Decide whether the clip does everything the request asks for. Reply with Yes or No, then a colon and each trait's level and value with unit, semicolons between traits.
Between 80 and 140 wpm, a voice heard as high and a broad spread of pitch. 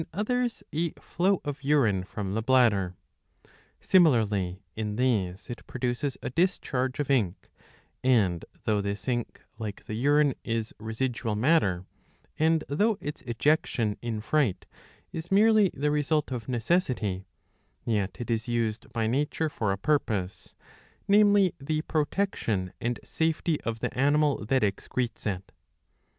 No: slow, 135 wpm; low, 125 Hz; wide, 6.0 semitones